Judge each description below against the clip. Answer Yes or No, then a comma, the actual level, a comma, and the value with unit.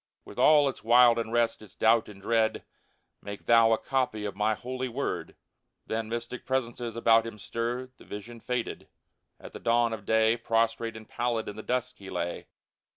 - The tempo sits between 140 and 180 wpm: No, average, 190 wpm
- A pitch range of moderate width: No, narrow, 1.5 semitones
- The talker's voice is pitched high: No, low, 115 Hz